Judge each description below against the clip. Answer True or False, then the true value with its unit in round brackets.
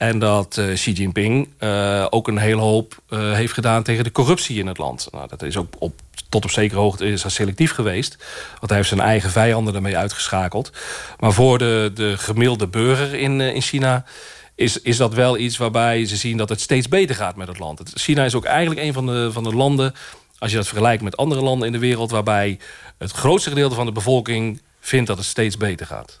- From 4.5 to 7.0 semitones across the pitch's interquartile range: False (3.4 semitones)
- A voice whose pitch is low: True (115 Hz)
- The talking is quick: True (225 wpm)